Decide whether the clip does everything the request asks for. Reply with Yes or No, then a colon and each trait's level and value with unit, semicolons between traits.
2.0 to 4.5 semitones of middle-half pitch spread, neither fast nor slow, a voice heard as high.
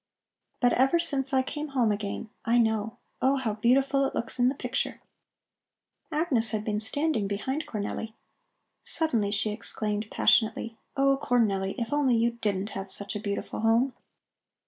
Yes: average, 4.2 semitones; average, 155 wpm; high, 230 Hz